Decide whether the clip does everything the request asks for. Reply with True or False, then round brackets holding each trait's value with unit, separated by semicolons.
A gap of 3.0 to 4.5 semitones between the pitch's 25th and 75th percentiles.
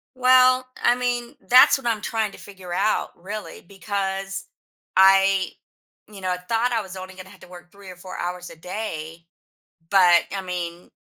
True (3.5 semitones)